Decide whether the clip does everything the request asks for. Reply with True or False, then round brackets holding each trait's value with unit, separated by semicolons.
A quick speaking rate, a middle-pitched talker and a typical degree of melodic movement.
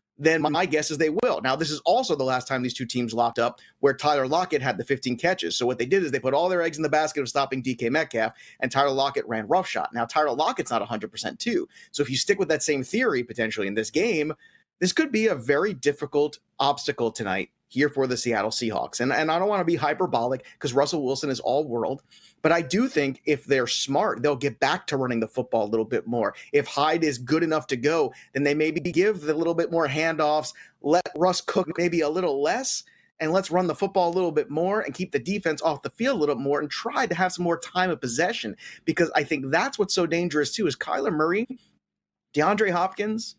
True (240 wpm; 150 Hz; 4.1 semitones)